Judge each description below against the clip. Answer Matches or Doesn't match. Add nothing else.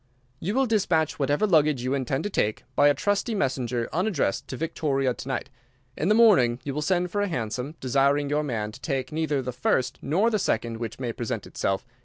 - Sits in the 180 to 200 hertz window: Doesn't match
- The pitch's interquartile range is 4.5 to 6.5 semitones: Matches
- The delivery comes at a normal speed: Doesn't match